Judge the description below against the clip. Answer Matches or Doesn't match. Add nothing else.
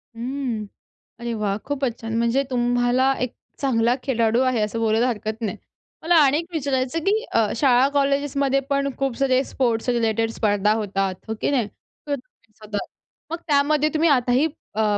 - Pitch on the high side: Matches